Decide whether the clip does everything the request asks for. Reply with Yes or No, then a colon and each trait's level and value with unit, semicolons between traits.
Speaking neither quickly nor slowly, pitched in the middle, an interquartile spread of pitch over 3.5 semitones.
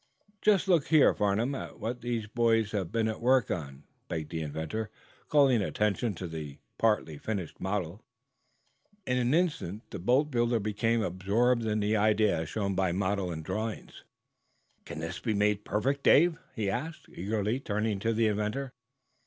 No: average, 165 wpm; low, 110 Hz; average, 3.9 semitones